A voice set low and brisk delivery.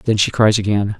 Yes: low, 105 Hz; fast, 240 wpm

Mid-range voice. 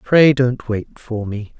No: low, 120 Hz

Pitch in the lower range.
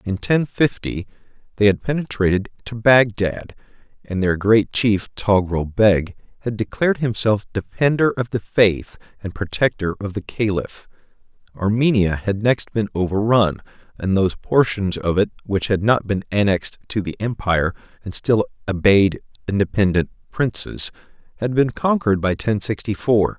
Yes: low, 105 Hz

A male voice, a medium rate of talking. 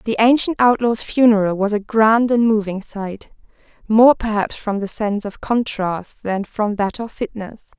No: female; average, 170 wpm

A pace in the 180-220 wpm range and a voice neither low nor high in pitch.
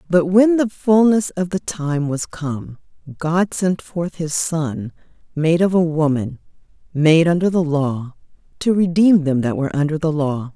No: average, 170 wpm; medium, 165 Hz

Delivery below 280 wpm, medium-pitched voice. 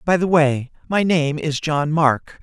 Yes: average, 200 wpm; medium, 155 Hz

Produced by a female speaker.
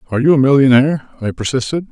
No: male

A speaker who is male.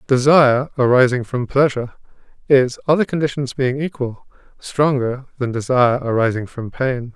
Yes: male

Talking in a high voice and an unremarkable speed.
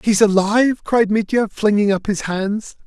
Yes: high, 210 Hz; average, 170 wpm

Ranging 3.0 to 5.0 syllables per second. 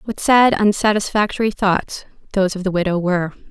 No: 5.5 syllables/s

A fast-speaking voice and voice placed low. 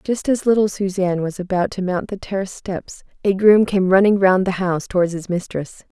No: fast, 210 wpm; high, 190 Hz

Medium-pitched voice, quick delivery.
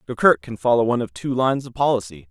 No: low, 115 Hz; fast, 235 wpm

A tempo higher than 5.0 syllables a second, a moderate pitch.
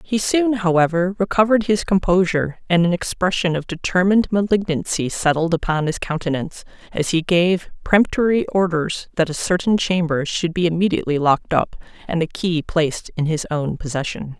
Yes: 5.5 syllables/s; medium, 175 Hz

